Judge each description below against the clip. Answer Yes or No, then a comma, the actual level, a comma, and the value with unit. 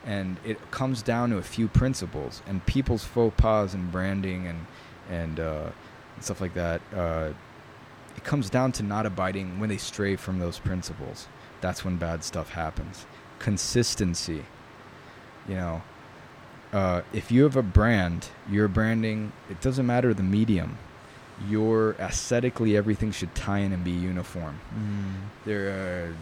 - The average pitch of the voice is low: Yes, low, 100 Hz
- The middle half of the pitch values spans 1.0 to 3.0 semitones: No, average, 3.8 semitones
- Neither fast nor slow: Yes, average, 155 wpm